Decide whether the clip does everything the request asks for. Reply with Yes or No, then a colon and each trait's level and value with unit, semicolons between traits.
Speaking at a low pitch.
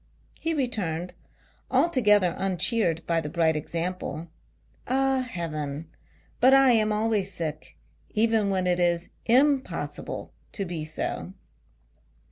No: high, 190 Hz